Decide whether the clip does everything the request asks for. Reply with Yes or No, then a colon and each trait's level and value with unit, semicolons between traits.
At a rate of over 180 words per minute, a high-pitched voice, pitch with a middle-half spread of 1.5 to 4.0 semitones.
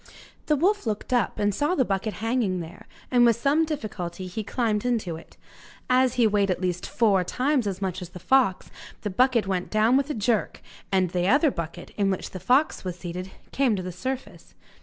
No: fast, 205 wpm; high, 215 Hz; wide, 5.5 semitones